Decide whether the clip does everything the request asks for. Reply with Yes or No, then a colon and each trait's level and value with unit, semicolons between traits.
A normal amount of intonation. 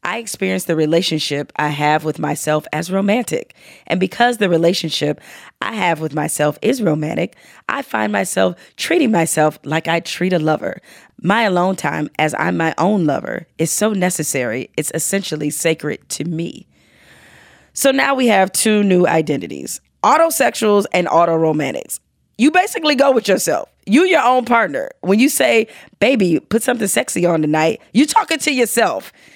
No: wide, 6.4 semitones